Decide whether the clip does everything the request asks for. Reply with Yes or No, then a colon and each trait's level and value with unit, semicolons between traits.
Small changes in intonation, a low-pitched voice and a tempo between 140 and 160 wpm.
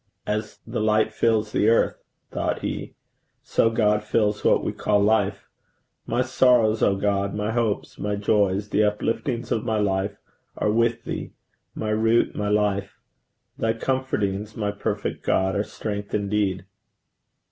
Yes: narrow, 1.6 semitones; low, 105 Hz; average, 145 wpm